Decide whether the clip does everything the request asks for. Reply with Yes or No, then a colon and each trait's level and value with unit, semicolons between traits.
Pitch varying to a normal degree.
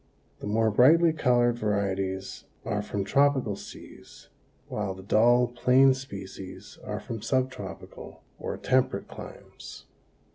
Yes: average, 4.5 semitones